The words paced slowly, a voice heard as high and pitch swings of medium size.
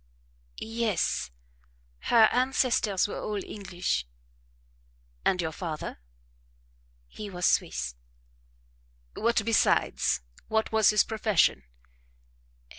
Yes: slow, 85 wpm; high, 205 Hz; average, 4.8 semitones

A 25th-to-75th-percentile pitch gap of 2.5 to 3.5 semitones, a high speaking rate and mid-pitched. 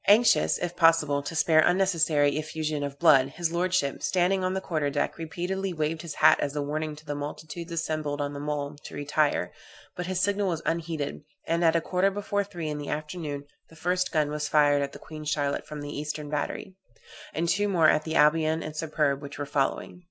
Yes: average, 2.9 semitones; fast, 210 wpm; medium, 155 Hz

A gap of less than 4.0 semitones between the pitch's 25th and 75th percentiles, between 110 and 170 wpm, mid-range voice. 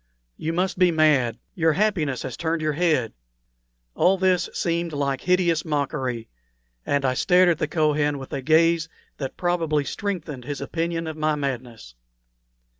Yes: average, 3.5 semitones; average, 155 wpm; medium, 155 Hz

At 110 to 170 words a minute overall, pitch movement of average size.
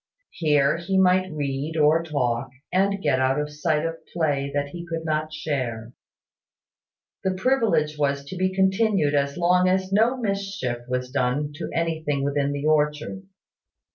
Yes: average, 155 wpm; average, 4.6 semitones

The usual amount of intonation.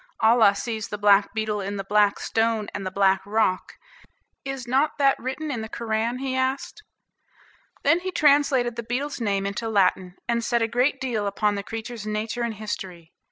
Yes: average, 3.5 semitones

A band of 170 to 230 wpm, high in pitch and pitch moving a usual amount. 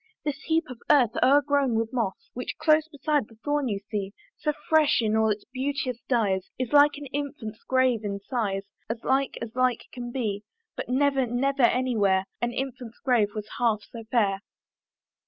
Yes: average, 180 wpm; high, 245 Hz; average, 4.1 semitones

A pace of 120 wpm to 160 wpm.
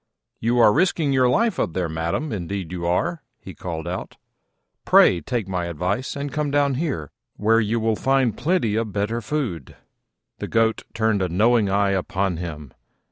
No: average, 175 wpm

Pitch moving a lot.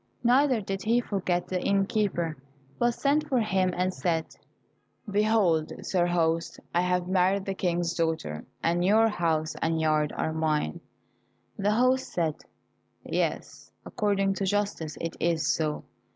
No: average, 4.0 semitones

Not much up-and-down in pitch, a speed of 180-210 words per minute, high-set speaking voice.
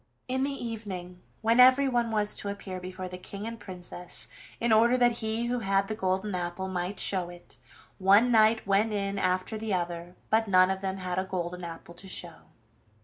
No: average, 3.4 semitones; average, 195 wpm; high, 195 Hz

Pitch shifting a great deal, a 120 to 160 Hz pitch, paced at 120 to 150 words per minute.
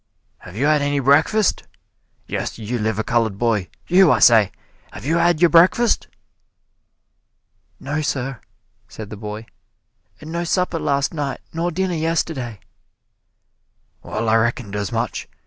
Yes: wide, 6.9 semitones; medium, 140 Hz; average, 140 wpm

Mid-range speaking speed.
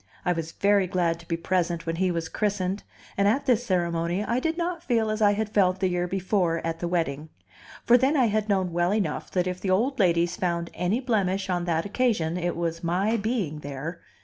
No: fast, 220 wpm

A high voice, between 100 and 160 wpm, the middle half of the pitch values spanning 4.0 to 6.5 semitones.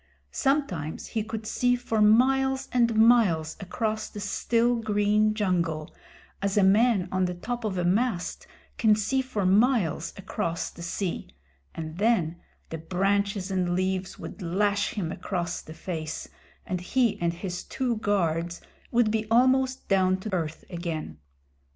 Yes: high, 200 Hz; average, 150 wpm; average, 4.4 semitones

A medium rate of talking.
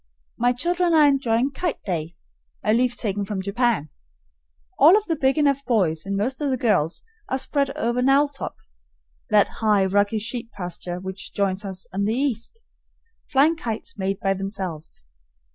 Yes: average, 160 wpm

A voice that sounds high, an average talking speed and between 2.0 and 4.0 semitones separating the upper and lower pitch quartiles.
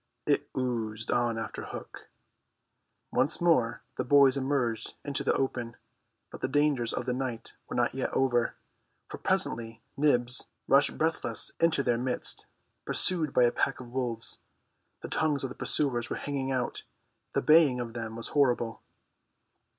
No: low, 125 Hz; average, 155 wpm; average, 2.9 semitones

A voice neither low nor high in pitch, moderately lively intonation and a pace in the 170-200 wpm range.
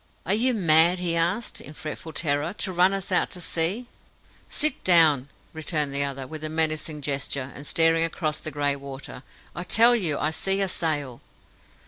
Yes: medium, 160 Hz; average, 3.7 semitones; average, 180 wpm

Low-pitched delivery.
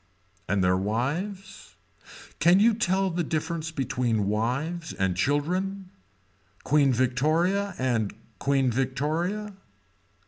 No: medium, 150 Hz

